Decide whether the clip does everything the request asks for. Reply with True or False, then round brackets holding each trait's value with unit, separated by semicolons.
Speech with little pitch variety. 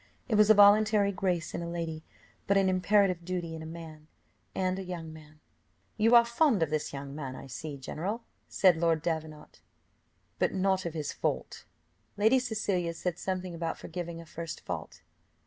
False (3.8 semitones)